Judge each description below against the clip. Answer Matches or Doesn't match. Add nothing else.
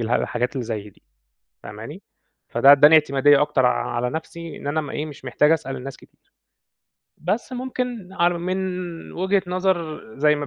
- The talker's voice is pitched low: Doesn't match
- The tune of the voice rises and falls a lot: Doesn't match